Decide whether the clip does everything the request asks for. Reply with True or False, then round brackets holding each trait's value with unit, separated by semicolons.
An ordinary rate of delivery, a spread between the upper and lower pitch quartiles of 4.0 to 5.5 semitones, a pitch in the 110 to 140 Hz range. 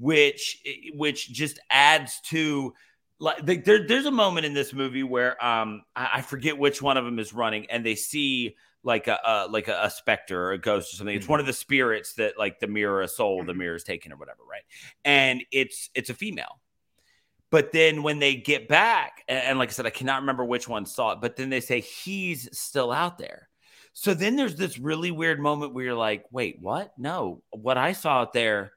False (220 wpm; 4.6 semitones; 135 Hz)